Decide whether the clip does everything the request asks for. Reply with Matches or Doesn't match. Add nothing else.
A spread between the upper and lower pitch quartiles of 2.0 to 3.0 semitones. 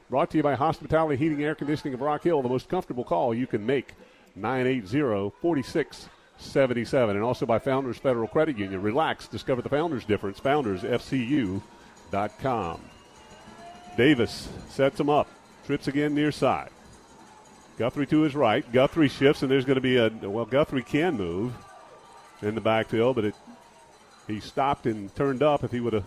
Doesn't match